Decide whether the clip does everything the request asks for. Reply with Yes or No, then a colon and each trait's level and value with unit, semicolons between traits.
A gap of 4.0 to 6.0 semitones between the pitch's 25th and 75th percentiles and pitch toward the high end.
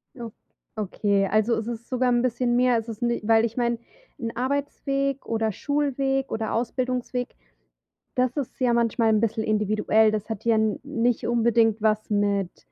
No: narrow, 2.4 semitones; high, 230 Hz